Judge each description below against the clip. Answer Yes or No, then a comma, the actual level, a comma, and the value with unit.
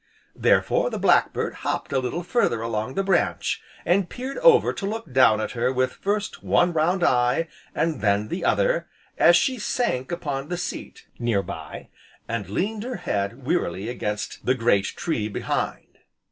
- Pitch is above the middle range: No, low, 135 Hz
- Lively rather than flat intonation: Yes, wide, 8.6 semitones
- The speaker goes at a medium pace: Yes, average, 170 wpm